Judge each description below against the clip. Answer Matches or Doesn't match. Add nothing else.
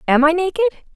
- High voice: Matches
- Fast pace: Doesn't match